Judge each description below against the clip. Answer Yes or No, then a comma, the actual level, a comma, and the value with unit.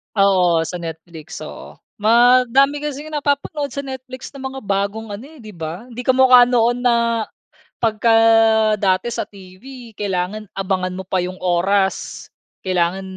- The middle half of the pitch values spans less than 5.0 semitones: No, average, 5.3 semitones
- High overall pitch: Yes, high, 215 Hz